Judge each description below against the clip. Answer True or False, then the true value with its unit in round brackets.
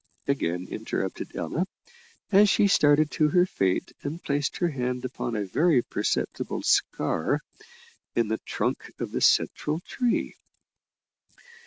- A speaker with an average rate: False (130 wpm)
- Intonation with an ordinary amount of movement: False (6.4 semitones)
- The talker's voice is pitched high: False (145 Hz)